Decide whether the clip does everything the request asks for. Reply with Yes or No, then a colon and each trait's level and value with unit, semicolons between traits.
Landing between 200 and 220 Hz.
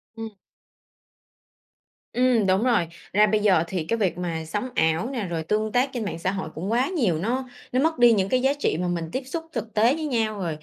Yes: high, 215 Hz